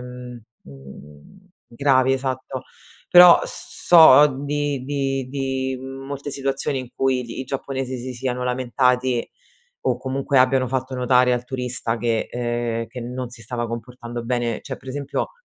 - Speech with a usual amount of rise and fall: No, narrow, 1.8 semitones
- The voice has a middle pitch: No, low, 130 Hz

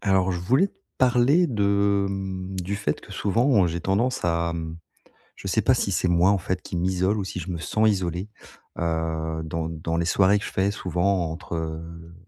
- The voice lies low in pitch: Yes, very low, 95 Hz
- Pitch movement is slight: No, average, 3.2 semitones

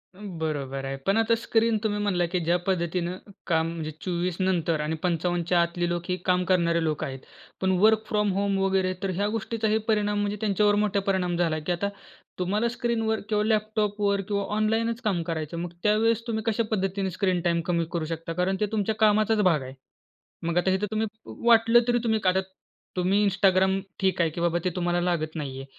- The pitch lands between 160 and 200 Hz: Yes, high, 190 Hz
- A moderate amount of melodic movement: Yes, average, 3.6 semitones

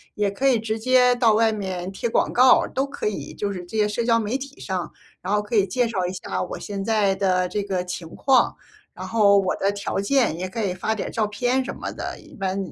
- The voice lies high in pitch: Yes, high, 210 Hz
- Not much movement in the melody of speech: No, average, 3.4 semitones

